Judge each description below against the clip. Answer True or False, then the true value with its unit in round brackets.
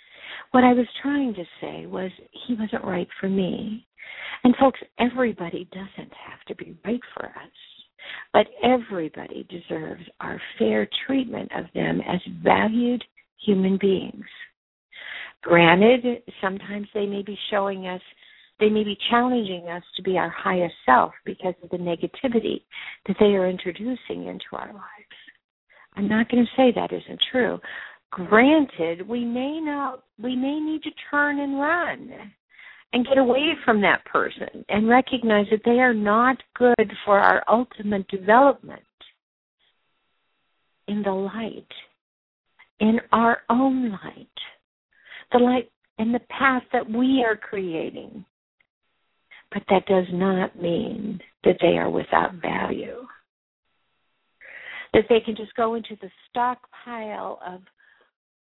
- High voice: True (220 Hz)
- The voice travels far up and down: False (4.4 semitones)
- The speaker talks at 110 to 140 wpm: True (135 wpm)